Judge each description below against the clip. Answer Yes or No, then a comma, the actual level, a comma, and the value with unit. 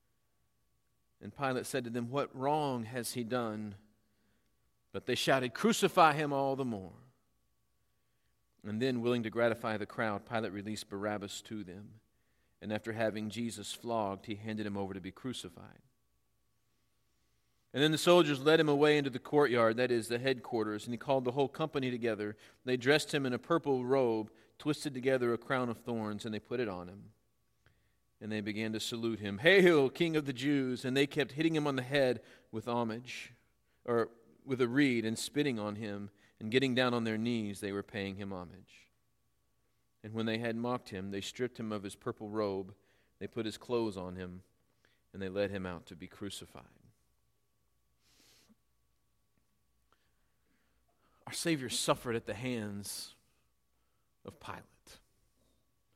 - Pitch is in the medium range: No, low, 115 Hz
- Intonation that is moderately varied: Yes, average, 3.5 semitones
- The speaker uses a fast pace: No, average, 170 wpm